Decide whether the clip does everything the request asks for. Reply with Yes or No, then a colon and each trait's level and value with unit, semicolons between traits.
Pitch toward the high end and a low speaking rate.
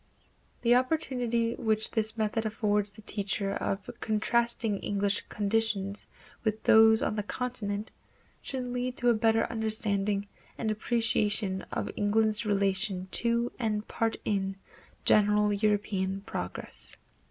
Yes: high, 215 Hz; slow, 120 wpm